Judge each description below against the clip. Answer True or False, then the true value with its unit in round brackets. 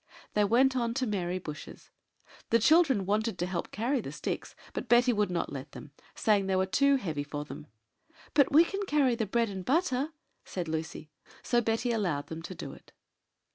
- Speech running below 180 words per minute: False (200 wpm)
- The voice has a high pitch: True (210 Hz)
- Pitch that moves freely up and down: True (6.1 semitones)